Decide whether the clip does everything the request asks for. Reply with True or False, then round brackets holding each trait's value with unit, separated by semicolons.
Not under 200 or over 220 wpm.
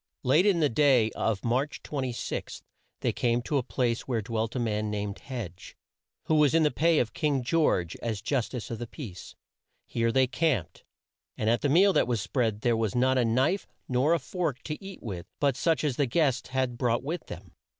True (205 wpm)